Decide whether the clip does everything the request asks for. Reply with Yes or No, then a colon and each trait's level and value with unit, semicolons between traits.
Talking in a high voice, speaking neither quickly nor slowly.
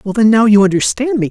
No: high, 210 Hz; fast, 275 wpm